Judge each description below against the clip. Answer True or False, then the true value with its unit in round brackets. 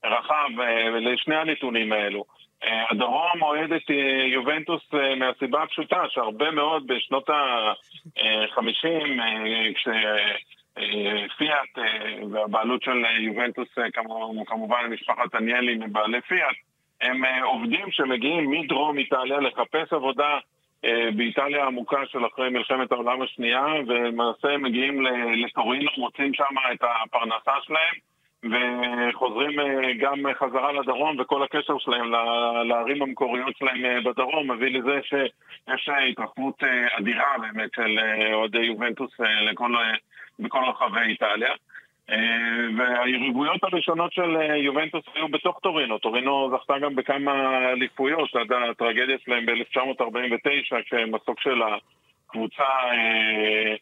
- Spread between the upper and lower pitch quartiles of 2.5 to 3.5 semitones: True (3.2 semitones)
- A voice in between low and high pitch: False (125 Hz)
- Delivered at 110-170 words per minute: False (100 wpm)